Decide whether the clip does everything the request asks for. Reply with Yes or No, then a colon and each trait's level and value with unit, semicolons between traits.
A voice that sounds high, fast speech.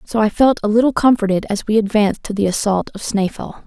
Yes: high, 215 Hz; fast, 230 wpm